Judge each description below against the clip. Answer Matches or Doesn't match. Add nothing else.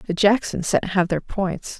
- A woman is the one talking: Matches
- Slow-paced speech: Doesn't match